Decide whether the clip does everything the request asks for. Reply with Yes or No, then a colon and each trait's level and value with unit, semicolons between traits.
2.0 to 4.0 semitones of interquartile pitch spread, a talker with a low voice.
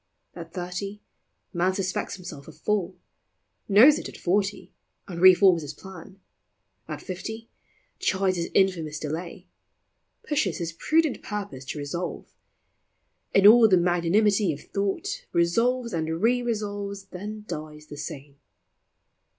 No: average, 3.7 semitones; medium, 185 Hz